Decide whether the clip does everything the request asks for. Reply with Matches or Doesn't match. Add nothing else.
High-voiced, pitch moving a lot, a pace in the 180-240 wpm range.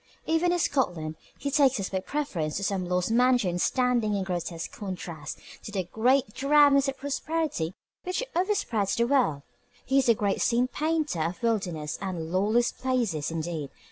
Doesn't match